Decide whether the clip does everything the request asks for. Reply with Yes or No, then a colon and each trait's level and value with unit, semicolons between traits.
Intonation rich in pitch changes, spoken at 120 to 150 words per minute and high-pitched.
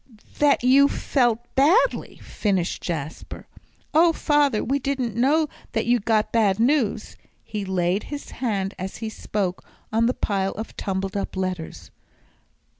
Yes: wide, 5.8 semitones; average, 145 wpm; high, 225 Hz